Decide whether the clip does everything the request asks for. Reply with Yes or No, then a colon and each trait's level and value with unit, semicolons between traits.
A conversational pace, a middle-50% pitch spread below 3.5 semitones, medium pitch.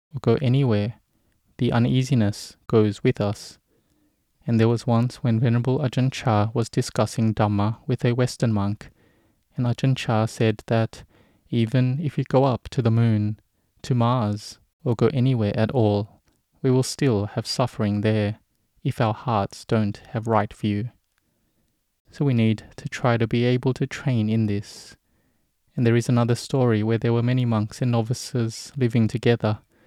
No: average, 165 wpm; average, 2.8 semitones; low, 115 Hz